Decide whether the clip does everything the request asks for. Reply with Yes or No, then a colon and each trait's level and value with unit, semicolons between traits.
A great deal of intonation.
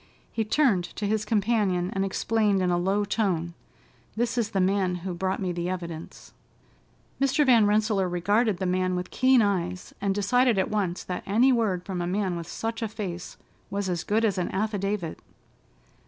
No: average, 3.2 semitones